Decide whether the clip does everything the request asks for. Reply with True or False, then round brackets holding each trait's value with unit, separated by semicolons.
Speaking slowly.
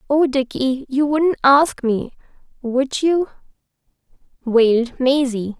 True (95 wpm)